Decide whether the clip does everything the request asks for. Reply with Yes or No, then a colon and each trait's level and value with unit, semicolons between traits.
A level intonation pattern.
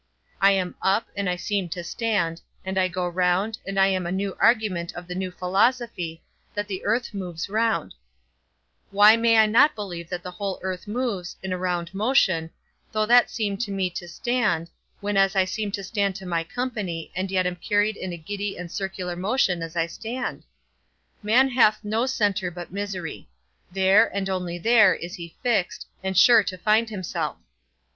No: average, 3.2 semitones